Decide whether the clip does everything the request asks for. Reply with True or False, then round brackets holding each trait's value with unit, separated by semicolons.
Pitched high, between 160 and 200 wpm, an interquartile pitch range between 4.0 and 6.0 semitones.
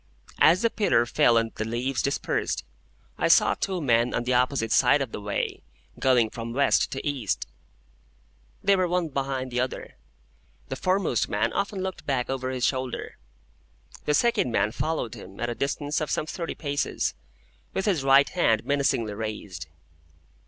False (130 Hz; 165 wpm; 4.7 semitones)